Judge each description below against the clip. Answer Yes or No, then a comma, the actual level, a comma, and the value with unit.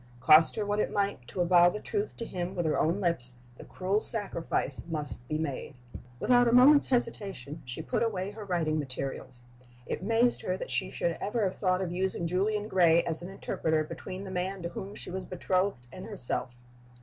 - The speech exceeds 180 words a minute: Yes, average, 200 wpm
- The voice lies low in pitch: No, medium, 185 Hz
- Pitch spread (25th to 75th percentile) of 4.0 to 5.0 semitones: Yes, average, 4.4 semitones